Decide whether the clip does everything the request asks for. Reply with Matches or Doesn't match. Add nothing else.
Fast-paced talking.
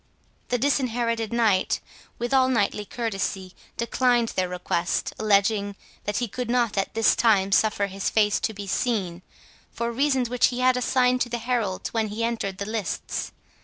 Doesn't match